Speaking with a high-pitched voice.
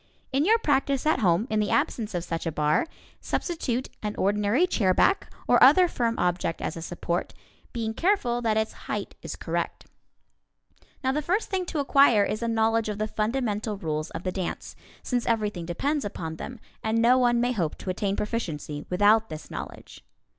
Yes: high, 220 Hz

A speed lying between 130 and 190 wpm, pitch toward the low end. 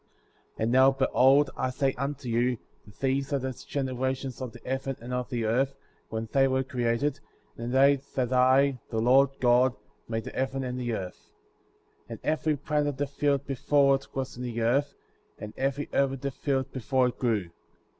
No: average, 200 wpm; low, 130 Hz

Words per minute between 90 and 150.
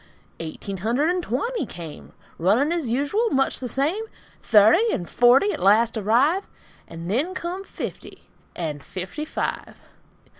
Yes: average, 140 wpm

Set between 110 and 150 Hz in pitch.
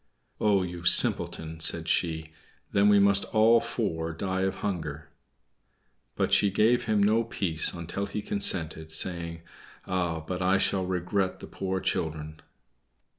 No: very low, 90 Hz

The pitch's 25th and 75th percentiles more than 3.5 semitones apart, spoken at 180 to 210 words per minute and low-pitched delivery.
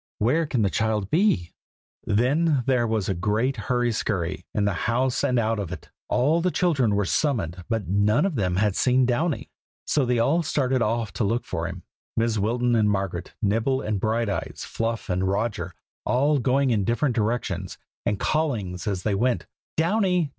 Yes: average, 4.5 semitones; average, 185 wpm; low, 115 Hz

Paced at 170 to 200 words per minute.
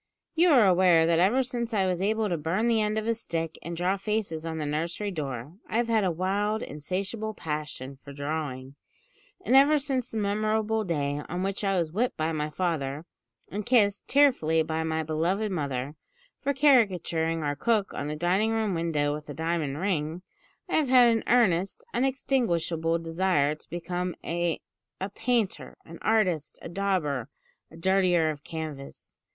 Yes: average, 175 wpm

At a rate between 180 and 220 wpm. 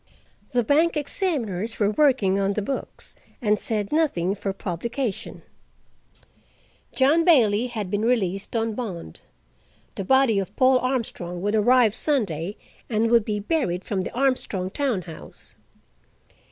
No: slow, 135 wpm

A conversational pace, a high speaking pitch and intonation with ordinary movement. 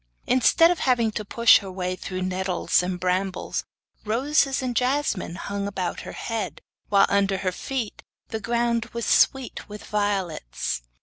Yes: average, 150 wpm; high, 205 Hz; average, 4.3 semitones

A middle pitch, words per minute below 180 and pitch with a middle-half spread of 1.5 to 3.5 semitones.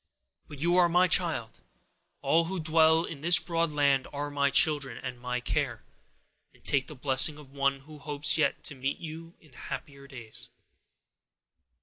Yes: medium, 145 Hz; average, 165 wpm; average, 3.0 semitones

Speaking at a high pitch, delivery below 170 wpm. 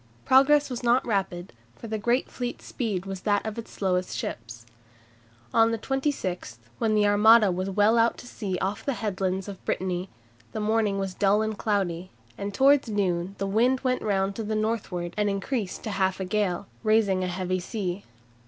No: high, 205 Hz; average, 185 wpm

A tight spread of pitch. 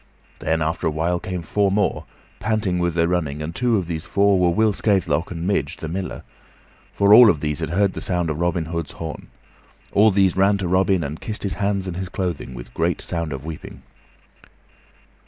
No: average, 3.4 semitones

